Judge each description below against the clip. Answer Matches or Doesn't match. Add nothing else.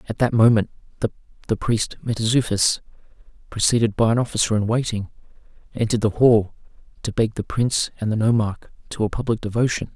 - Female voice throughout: Doesn't match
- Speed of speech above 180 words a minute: Doesn't match